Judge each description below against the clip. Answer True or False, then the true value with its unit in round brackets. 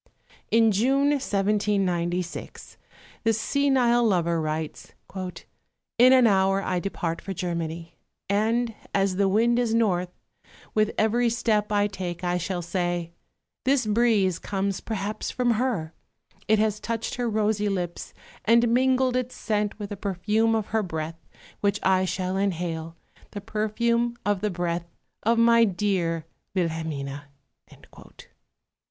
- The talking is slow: True (130 wpm)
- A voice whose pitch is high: True (205 Hz)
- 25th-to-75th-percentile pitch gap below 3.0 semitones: False (4.3 semitones)